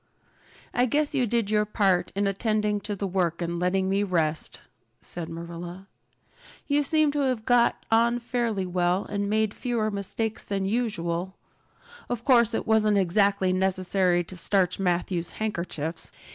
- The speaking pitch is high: Yes, high, 200 Hz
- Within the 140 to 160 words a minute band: Yes, average, 150 wpm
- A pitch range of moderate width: Yes, average, 3.8 semitones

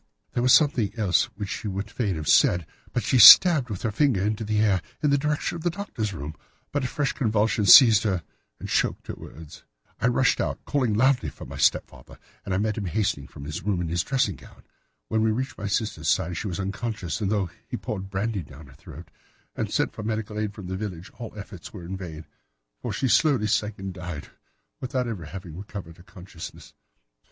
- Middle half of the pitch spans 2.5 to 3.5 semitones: No, average, 4.2 semitones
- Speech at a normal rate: No, fast, 215 wpm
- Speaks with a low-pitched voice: Yes, low, 105 Hz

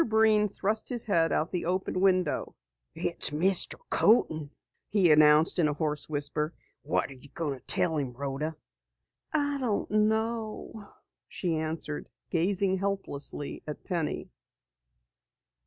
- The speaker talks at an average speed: No, slow, 130 wpm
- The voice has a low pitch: No, medium, 170 Hz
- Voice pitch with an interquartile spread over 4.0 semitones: Yes, wide, 5.5 semitones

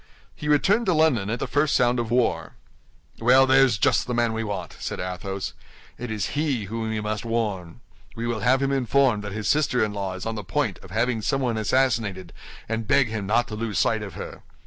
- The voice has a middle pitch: No, low, 115 Hz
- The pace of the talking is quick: Yes, fast, 215 wpm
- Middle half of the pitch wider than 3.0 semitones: Yes, average, 3.8 semitones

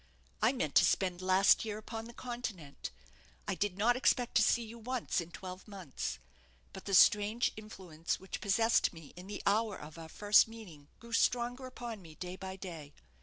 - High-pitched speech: Yes, high, 205 Hz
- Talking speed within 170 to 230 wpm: Yes, average, 185 wpm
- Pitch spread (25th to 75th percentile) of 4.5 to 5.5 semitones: No, average, 4.0 semitones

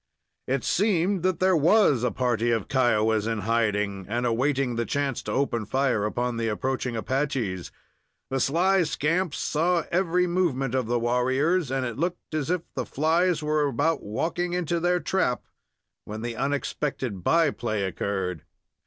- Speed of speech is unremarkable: Yes, average, 160 wpm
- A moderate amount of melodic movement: No, wide, 6.3 semitones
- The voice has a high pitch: No, low, 135 Hz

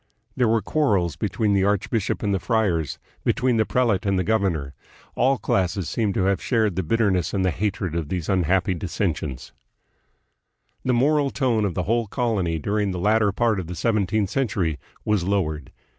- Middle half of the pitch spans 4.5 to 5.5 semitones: No, average, 3.7 semitones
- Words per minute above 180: No, average, 175 wpm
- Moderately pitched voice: No, low, 100 Hz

